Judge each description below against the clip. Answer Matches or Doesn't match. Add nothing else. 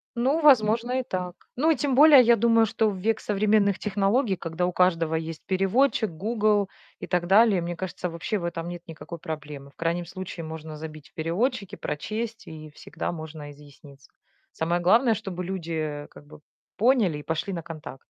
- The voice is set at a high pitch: Doesn't match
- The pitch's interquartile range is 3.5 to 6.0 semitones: Matches